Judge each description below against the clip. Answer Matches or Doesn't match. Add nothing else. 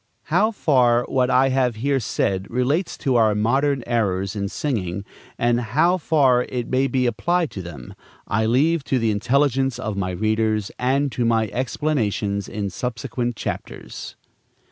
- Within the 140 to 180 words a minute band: Matches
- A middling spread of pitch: Matches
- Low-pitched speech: Matches